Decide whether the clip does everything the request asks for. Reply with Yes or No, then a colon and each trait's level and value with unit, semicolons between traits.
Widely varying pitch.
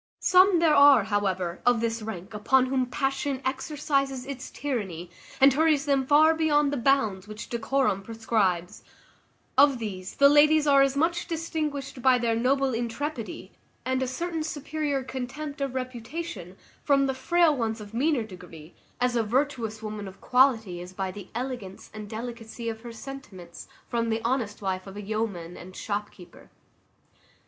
No: average, 4.9 semitones